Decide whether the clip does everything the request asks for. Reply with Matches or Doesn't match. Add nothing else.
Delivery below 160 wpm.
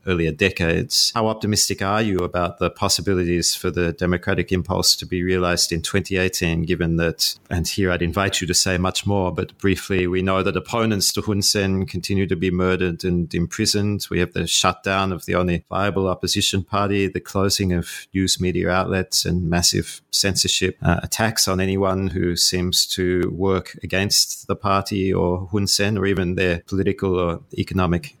Doesn't match